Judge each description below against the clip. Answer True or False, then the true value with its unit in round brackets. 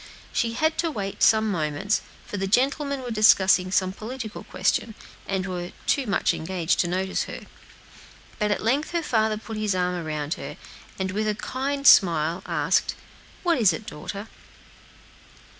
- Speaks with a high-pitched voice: True (205 Hz)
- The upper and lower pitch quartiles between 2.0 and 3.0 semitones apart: False (4.2 semitones)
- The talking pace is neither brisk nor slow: True (160 wpm)